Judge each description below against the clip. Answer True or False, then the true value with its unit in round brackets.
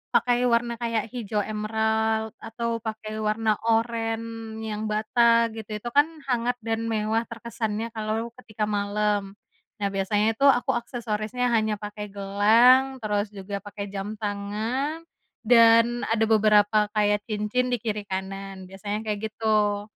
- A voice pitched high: True (220 Hz)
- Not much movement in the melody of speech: True (1.8 semitones)